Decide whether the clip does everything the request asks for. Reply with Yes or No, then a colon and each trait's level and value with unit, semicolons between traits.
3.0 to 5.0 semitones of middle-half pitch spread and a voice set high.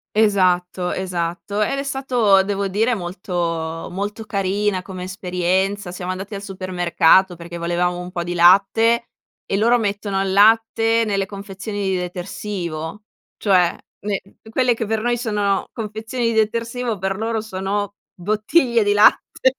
Yes: average, 3.3 semitones; high, 200 Hz